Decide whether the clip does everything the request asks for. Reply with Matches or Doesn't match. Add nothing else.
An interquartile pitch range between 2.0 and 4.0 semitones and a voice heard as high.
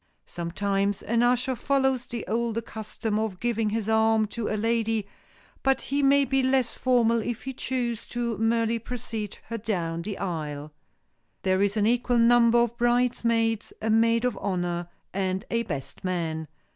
Matches